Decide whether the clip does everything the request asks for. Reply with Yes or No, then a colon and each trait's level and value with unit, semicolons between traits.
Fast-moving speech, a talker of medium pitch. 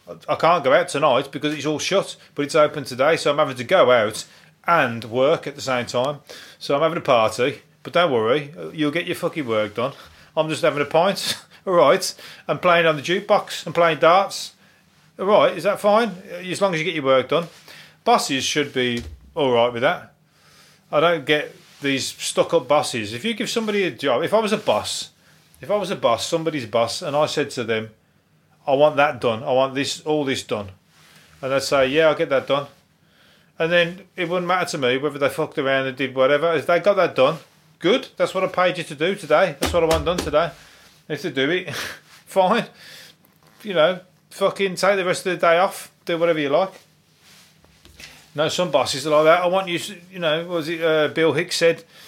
Yes: fast, 225 wpm; medium, 160 Hz